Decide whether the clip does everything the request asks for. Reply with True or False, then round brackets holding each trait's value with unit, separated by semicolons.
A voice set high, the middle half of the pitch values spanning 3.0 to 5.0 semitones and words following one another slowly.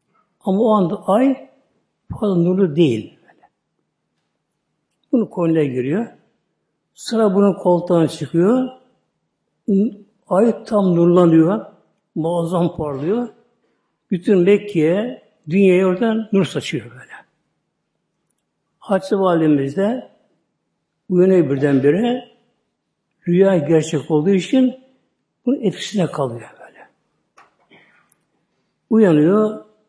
True (195 Hz; 4.1 semitones; 80 wpm)